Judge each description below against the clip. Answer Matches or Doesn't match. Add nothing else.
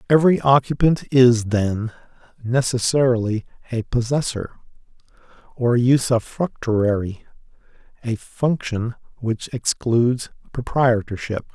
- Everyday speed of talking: Doesn't match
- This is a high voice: Doesn't match